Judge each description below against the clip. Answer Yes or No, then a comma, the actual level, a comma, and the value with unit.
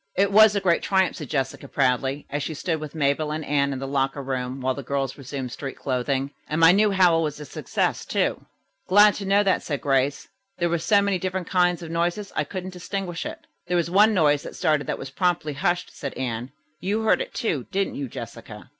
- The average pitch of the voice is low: No, medium, 155 Hz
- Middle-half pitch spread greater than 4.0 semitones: Yes, average, 5.2 semitones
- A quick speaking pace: Yes, fast, 225 wpm